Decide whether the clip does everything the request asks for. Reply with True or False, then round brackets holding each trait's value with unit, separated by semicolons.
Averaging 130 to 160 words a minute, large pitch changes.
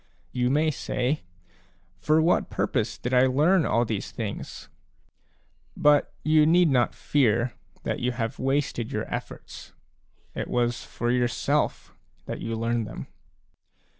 False (140 wpm; 4.3 semitones)